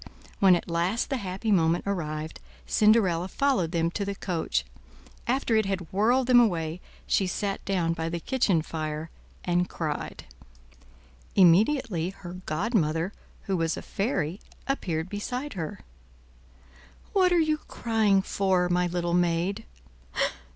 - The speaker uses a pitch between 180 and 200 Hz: Yes, medium, 185 Hz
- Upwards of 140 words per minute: No, slow, 135 wpm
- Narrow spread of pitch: No, average, 4.6 semitones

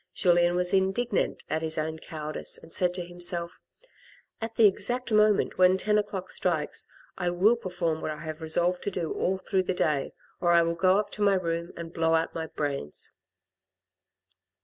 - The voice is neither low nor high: Yes, medium, 175 Hz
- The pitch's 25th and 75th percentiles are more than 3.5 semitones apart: No, average, 2.8 semitones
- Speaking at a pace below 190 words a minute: No, average, 195 wpm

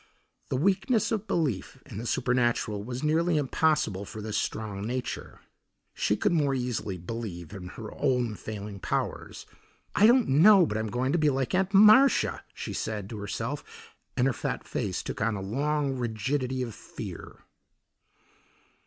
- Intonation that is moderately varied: No, wide, 6.0 semitones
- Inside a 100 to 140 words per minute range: No, average, 160 wpm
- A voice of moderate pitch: No, low, 125 Hz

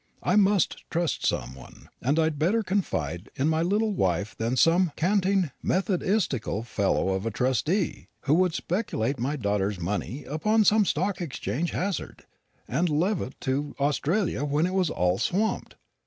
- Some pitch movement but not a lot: No, wide, 7.7 semitones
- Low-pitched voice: No, medium, 155 Hz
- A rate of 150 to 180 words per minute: Yes, average, 155 wpm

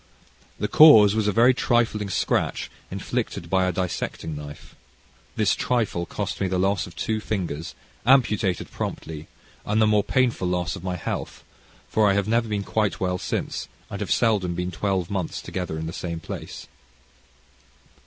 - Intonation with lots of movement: No, average, 3.5 semitones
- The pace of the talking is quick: No, average, 165 wpm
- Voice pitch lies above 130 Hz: No, very low, 95 Hz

